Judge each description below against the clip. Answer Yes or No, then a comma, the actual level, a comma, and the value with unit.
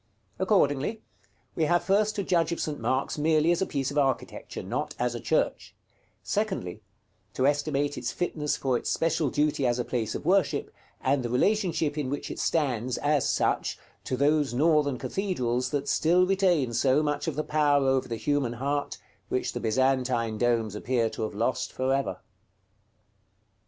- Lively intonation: No, average, 3.6 semitones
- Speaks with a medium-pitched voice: Yes, medium, 145 Hz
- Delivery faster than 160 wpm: Yes, average, 170 wpm